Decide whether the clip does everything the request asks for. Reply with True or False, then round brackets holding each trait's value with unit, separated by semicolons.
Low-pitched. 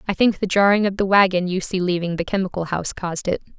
False (185 Hz)